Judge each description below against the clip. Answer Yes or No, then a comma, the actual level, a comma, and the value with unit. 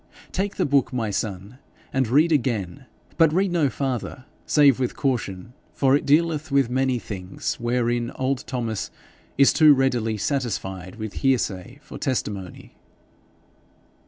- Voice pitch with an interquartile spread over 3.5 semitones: Yes, average, 4.2 semitones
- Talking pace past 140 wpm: No, slow, 135 wpm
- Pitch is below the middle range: Yes, low, 125 Hz